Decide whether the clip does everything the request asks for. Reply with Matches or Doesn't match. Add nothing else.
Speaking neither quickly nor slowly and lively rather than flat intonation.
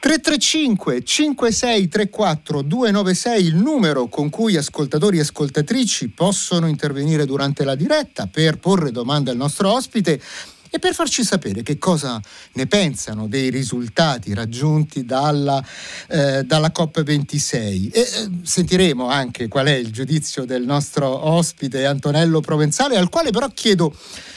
Matches